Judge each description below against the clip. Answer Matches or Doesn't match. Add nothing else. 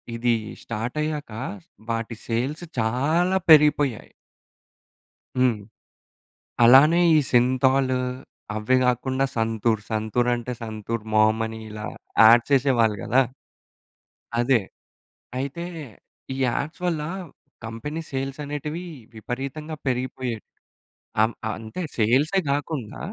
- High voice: Doesn't match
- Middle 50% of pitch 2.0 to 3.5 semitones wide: Doesn't match